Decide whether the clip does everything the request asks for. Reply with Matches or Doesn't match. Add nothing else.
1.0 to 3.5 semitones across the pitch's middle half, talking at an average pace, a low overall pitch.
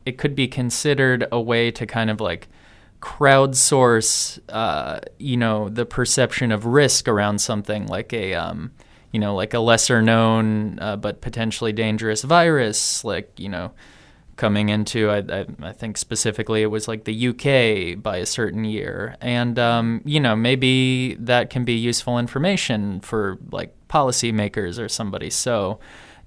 Matches